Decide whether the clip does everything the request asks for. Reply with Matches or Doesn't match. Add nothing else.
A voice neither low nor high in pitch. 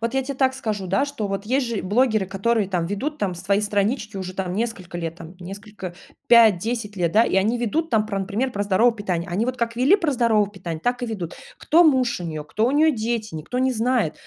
Doesn't match